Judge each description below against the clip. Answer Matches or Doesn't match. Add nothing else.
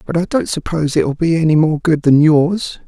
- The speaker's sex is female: Doesn't match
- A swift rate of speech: Matches